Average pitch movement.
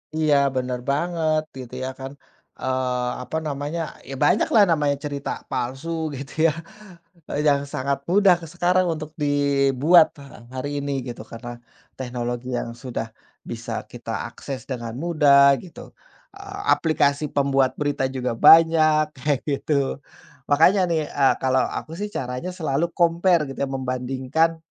Yes: average, 3.5 semitones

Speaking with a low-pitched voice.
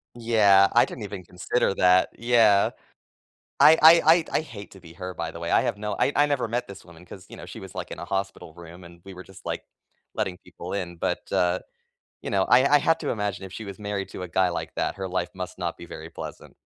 Yes: very low, 95 Hz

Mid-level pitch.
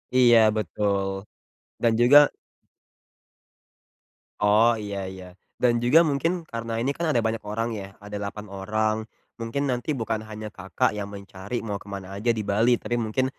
No: low, 110 Hz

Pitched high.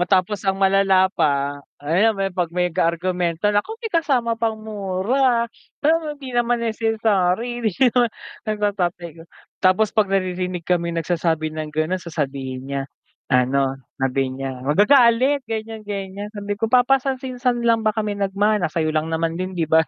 Yes: high, 195 Hz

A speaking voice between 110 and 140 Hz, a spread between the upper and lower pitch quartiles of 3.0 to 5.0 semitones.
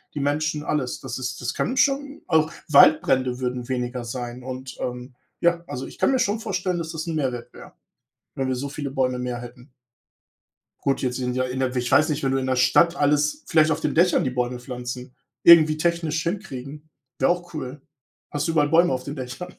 Yes: low, 135 Hz; average, 4.1 semitones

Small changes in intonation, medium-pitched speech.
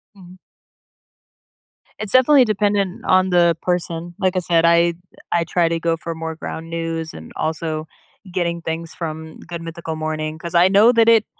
Yes: narrow, 2.3 semitones; medium, 170 Hz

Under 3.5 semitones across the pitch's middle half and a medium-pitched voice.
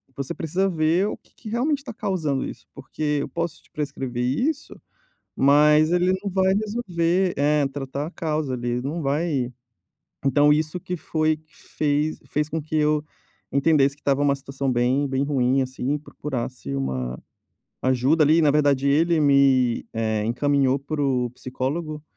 Yes: average, 3.1 semitones; medium, 145 Hz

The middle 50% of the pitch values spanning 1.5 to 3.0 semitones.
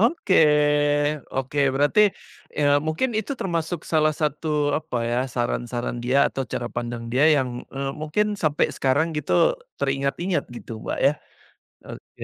No: average, 3.6 semitones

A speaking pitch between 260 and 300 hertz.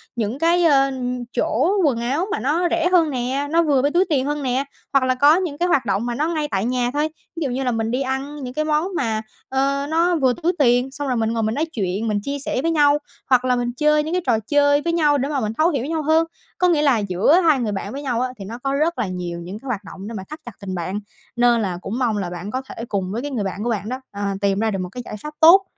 Yes: very high, 265 Hz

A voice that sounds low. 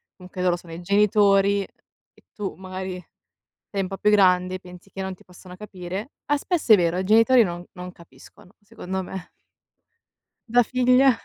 No: high, 190 Hz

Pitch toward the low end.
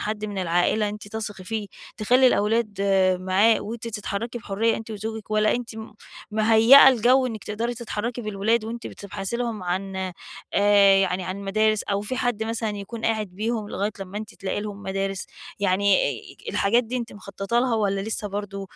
No: high, 210 Hz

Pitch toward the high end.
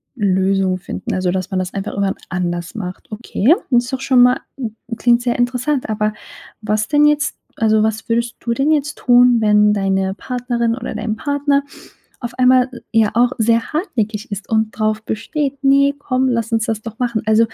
Yes: high, 230 Hz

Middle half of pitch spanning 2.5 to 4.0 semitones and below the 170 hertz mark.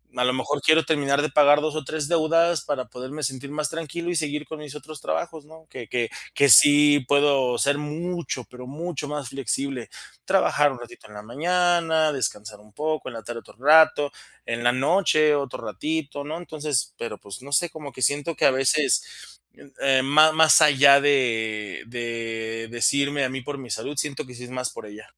Yes: average, 3.6 semitones; medium, 140 Hz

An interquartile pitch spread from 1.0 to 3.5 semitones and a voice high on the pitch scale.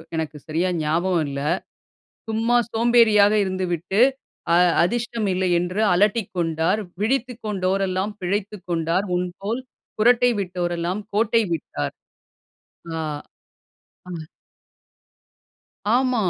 No: average, 4.2 semitones; high, 195 Hz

